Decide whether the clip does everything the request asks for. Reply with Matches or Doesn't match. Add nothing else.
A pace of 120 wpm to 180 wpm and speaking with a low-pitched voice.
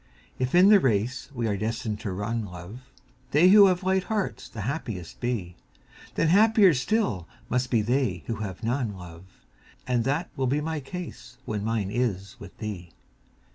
Matches